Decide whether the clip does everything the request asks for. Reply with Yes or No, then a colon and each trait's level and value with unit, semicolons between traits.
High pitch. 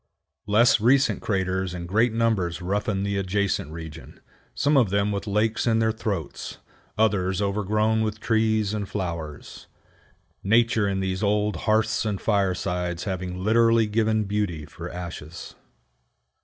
No: low, 100 Hz